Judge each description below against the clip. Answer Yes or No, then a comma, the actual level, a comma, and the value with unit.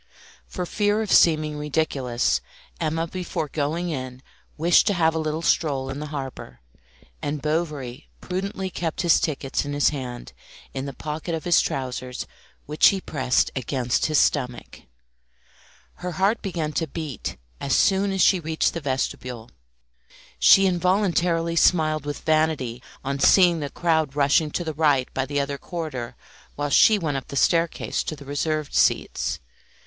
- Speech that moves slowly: No, average, 155 wpm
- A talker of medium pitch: Yes, medium, 155 Hz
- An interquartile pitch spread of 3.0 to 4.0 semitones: Yes, average, 3.5 semitones